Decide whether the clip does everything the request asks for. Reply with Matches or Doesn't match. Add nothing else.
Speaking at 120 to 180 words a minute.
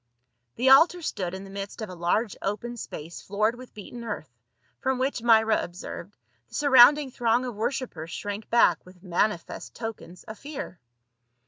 Matches